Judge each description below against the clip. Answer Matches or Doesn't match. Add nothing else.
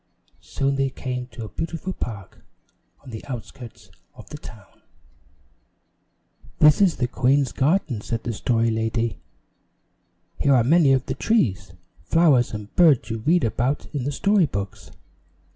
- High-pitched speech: Doesn't match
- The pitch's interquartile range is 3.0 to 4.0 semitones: Doesn't match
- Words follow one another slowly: Doesn't match